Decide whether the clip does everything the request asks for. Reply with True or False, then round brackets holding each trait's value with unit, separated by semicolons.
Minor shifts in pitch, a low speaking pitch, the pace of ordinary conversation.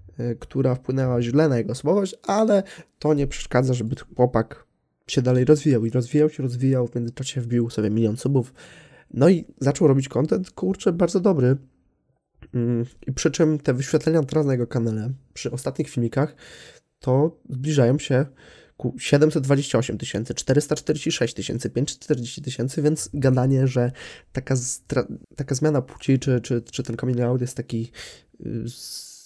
False (3.9 semitones; 130 Hz; 150 wpm)